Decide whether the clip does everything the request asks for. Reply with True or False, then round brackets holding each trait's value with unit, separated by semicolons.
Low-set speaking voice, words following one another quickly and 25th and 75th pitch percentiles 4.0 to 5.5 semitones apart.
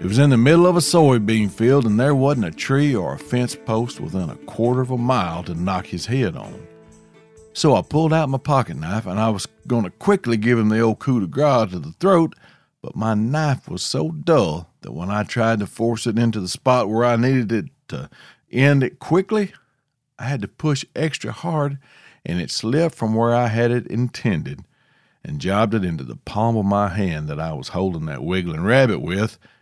True (120 Hz; 220 wpm; 4.7 semitones)